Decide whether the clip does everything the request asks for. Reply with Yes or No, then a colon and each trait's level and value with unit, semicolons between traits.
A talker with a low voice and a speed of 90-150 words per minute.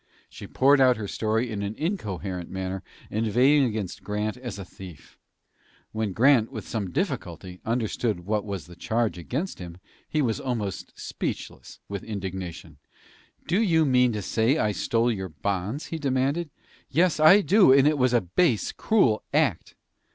No: low, 110 Hz; average, 160 wpm